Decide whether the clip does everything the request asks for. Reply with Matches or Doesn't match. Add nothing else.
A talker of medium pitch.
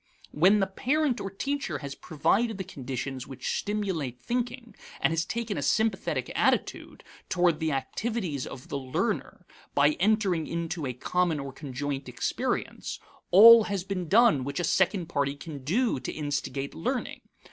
Matches